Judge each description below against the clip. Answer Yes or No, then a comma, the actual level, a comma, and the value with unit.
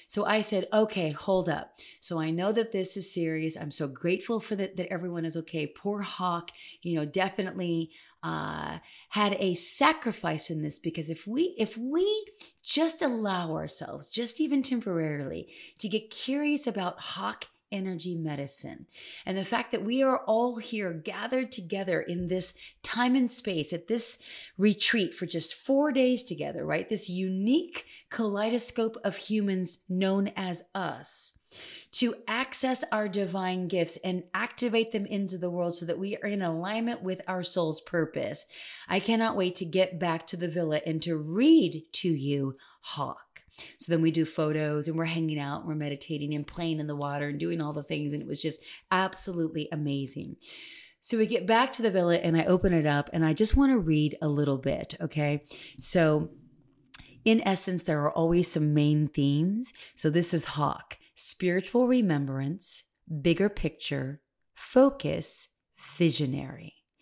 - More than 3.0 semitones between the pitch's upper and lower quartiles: Yes, average, 5.3 semitones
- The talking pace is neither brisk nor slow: Yes, average, 170 wpm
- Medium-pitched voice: Yes, medium, 180 Hz